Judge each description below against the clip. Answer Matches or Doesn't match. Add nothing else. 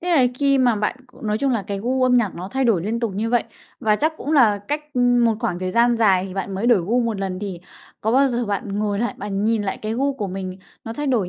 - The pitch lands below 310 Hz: Matches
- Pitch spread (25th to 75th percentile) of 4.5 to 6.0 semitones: Doesn't match